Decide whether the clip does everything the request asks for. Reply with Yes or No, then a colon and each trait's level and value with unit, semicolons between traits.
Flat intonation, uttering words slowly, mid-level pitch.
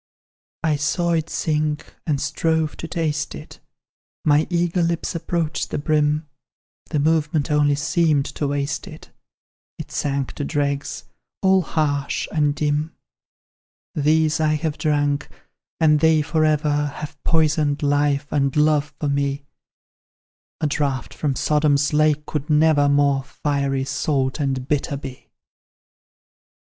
Yes: narrow, 1.6 semitones; slow, 130 wpm; medium, 150 Hz